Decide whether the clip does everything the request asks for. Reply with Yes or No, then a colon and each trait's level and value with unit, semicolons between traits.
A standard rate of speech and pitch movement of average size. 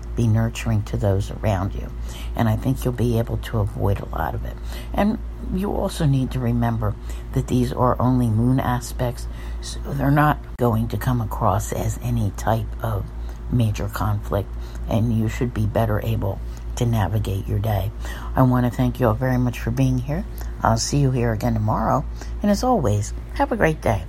Yes: average, 190 wpm; average, 3.8 semitones